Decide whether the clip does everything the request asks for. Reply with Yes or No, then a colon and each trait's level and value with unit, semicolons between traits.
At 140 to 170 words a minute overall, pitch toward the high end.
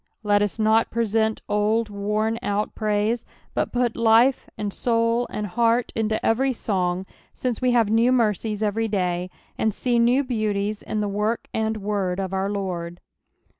Yes: average, 165 wpm; high, 215 Hz